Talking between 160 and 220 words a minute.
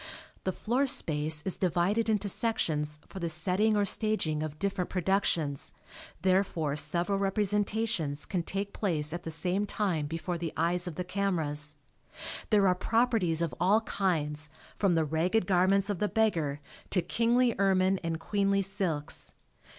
No: average, 150 wpm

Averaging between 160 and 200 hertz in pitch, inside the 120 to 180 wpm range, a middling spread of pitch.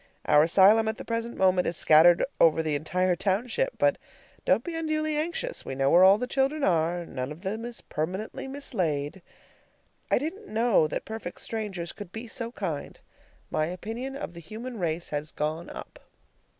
No: high, 190 Hz; average, 175 wpm; wide, 6.4 semitones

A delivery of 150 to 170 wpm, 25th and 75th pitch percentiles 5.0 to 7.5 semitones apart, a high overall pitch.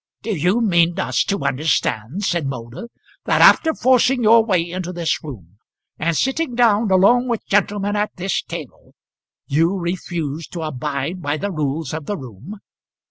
No: average, 160 wpm; wide, 5.6 semitones; medium, 175 Hz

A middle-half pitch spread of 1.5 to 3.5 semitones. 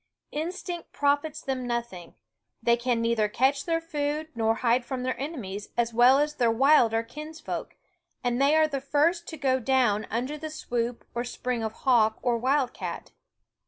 No: average, 4.1 semitones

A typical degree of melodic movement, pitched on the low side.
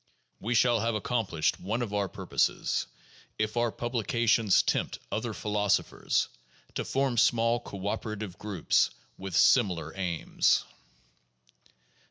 Yes: average, 3.2 semitones; low, 110 Hz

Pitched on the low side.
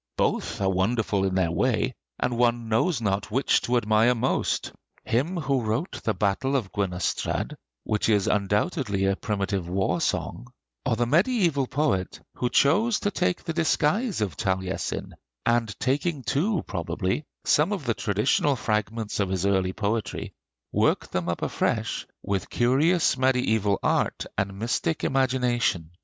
Yes: low, 115 Hz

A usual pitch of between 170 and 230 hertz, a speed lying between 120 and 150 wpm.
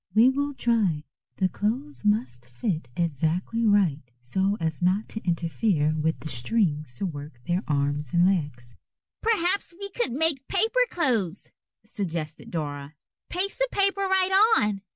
Yes: high, 190 Hz; average, 145 wpm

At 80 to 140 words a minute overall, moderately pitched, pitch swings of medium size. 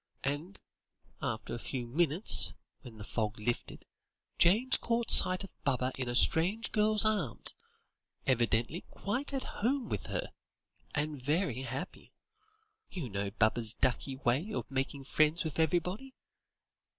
No: slow, 135 wpm; medium, 150 Hz; wide, 8.1 semitones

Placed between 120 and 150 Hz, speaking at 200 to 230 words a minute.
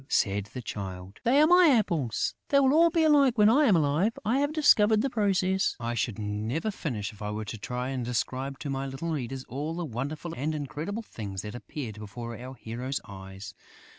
Yes: low, 135 Hz; fast, 205 wpm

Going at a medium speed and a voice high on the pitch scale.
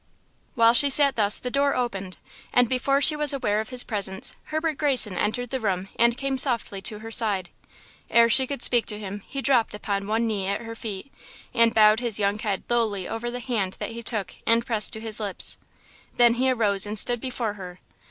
No: fast, 210 wpm; high, 230 Hz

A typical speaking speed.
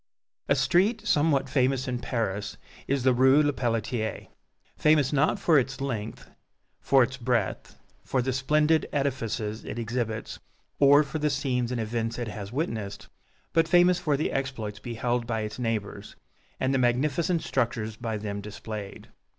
Yes: average, 150 wpm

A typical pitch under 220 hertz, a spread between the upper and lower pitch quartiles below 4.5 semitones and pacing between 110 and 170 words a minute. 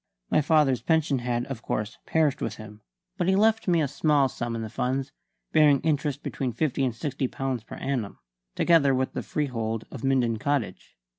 No: low, 135 Hz; average, 3.9 semitones; average, 190 wpm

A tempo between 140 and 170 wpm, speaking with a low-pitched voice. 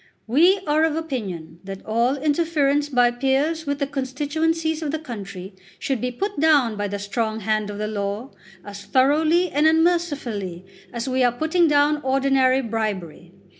No: average, 165 wpm; very high, 265 Hz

